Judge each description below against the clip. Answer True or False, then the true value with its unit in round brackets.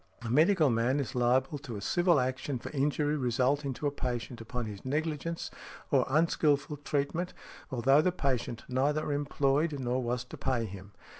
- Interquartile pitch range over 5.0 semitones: False (3.2 semitones)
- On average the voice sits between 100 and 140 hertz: True (135 Hz)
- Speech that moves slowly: False (165 wpm)